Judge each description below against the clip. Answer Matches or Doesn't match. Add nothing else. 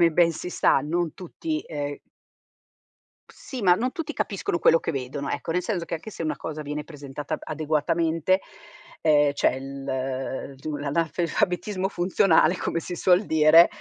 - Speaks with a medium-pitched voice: Matches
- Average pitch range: Matches